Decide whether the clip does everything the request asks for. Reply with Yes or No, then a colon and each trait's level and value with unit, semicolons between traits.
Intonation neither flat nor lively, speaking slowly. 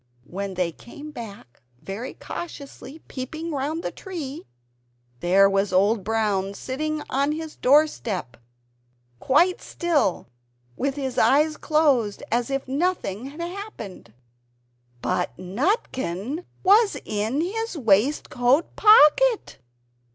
No: wide, 7.4 semitones; slow, 110 wpm